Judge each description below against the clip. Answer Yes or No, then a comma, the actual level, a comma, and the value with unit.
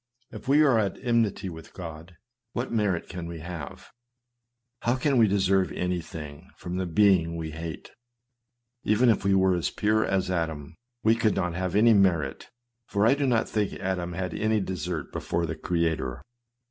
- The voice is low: Yes, very low, 95 Hz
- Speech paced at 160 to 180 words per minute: Yes, average, 170 wpm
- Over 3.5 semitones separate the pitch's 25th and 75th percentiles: Yes, average, 4.3 semitones